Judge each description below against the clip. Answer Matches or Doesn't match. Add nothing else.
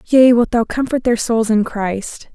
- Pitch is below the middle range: Doesn't match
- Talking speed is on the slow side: Doesn't match